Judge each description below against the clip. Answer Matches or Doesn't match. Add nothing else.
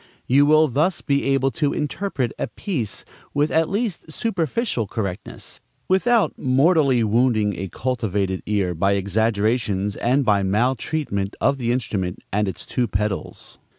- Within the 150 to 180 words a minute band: Doesn't match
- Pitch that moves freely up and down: Matches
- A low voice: Matches